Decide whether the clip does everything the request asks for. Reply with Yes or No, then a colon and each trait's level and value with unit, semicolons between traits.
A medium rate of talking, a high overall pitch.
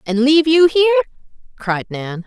Yes: average, 160 wpm; very high, 275 Hz